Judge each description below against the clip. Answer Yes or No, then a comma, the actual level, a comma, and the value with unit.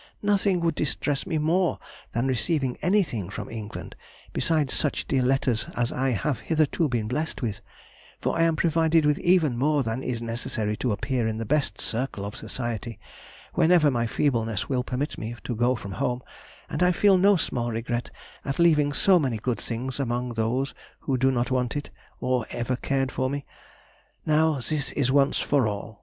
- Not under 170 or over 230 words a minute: Yes, average, 180 wpm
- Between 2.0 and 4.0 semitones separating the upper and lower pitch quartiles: No, average, 4.4 semitones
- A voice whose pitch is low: Yes, low, 130 Hz